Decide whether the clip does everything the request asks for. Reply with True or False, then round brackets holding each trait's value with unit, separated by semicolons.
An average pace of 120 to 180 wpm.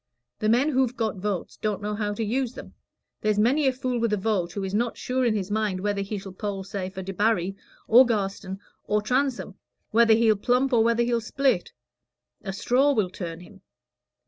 False (200 wpm)